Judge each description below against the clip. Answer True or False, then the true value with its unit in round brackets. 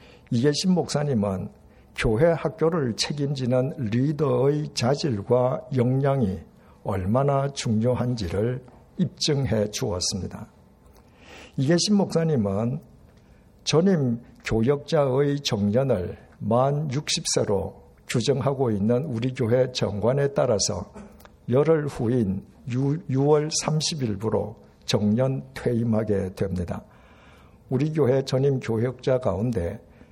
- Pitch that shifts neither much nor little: True (4.5 semitones)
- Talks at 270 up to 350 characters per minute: False (210 characters per minute)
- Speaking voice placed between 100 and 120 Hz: False (130 Hz)